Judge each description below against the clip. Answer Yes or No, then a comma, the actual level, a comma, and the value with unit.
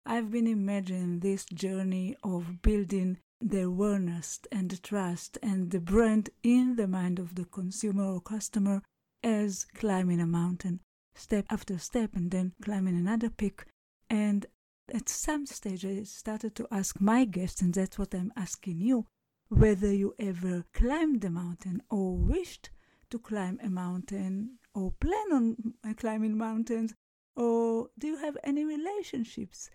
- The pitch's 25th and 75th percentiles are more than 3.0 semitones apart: Yes, average, 3.6 semitones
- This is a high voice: Yes, high, 205 Hz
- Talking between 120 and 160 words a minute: Yes, average, 150 wpm